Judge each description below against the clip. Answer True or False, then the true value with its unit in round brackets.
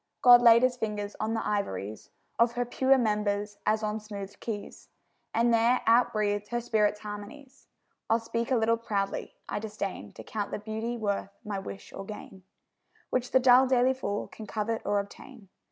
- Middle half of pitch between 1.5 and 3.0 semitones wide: True (2.6 semitones)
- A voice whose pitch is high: True (220 Hz)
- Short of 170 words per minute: False (180 wpm)